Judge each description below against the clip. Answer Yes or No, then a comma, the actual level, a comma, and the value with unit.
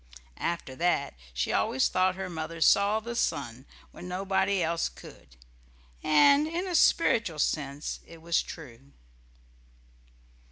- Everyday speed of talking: No, slow, 125 wpm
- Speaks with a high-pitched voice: No, medium, 170 Hz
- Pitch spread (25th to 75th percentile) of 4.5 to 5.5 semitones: Yes, average, 5.1 semitones